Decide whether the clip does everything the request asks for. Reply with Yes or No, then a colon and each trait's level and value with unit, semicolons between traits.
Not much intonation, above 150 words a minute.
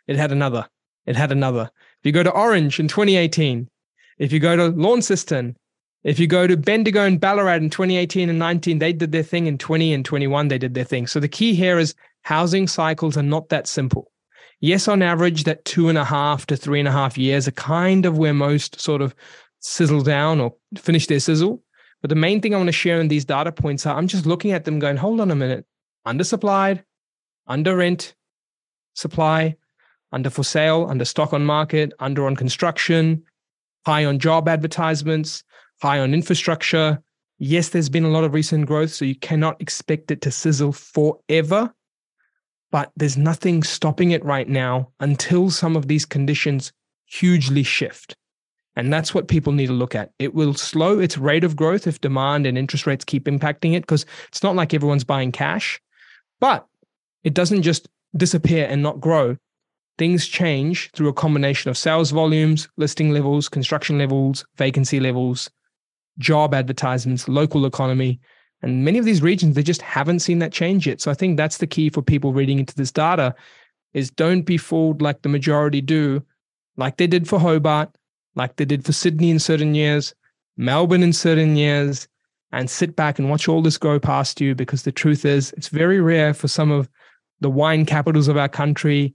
No: average, 3.0 semitones; average, 190 wpm